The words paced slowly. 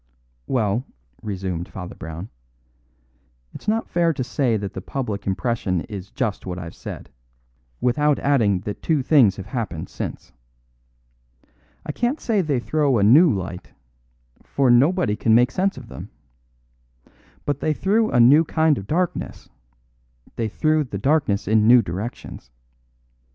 No: average, 145 wpm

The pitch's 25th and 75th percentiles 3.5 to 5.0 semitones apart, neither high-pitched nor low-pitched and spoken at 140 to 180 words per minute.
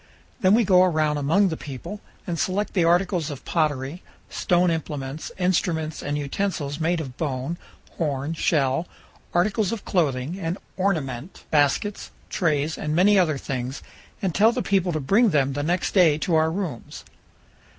Yes: average, 4.2 semitones; medium, 160 Hz; average, 160 wpm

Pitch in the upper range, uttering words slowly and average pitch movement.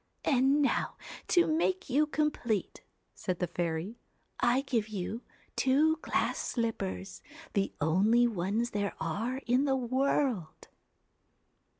No: high, 235 Hz; slow, 120 wpm; wide, 5.8 semitones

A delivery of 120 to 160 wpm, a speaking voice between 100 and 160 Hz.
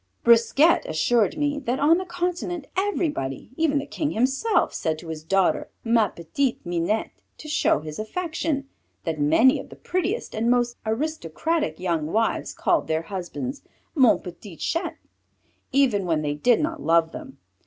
No: average, 155 wpm; high, 240 Hz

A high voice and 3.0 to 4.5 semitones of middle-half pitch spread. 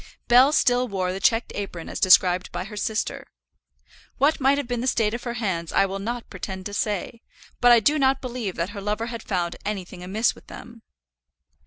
Yes: high, 220 Hz; average, 4.2 semitones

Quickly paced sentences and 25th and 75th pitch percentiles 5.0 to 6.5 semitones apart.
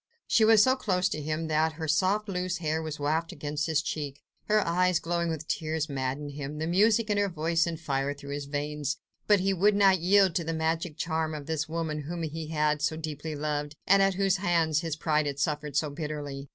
No: fast, 220 wpm; average, 3.2 semitones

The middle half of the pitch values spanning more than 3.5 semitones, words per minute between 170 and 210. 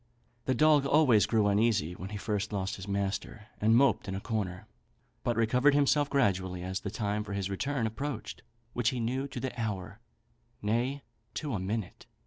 Yes: average, 4.6 semitones; average, 180 wpm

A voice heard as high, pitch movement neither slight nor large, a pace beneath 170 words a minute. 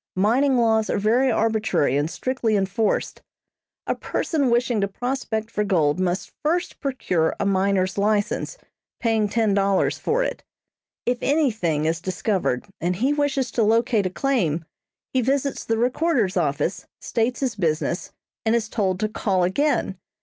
Yes: high, 220 Hz; average, 5.0 semitones; average, 150 wpm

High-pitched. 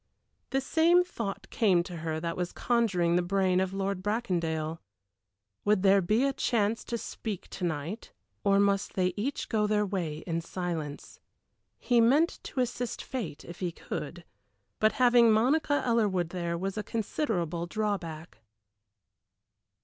Yes: high, 195 Hz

